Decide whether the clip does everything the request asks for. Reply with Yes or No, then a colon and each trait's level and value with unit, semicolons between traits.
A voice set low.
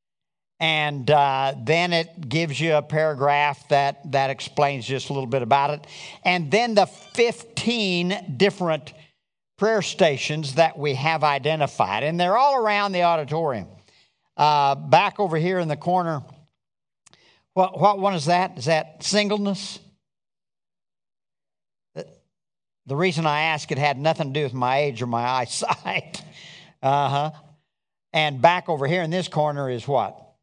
No: medium, 155 Hz